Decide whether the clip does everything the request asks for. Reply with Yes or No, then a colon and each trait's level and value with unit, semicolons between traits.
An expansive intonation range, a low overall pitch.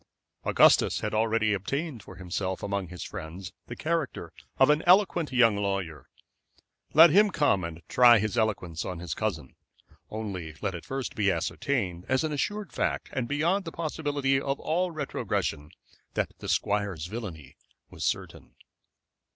Yes: wide, 7.9 semitones; low, 110 Hz